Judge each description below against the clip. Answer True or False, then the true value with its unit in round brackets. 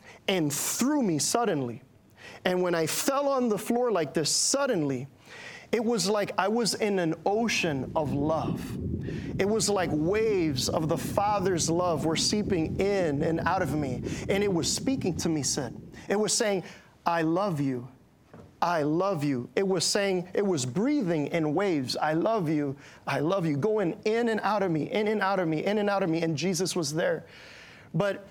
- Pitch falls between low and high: True (180 Hz)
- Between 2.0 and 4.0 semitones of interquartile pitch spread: False (5.1 semitones)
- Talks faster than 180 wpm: True (190 wpm)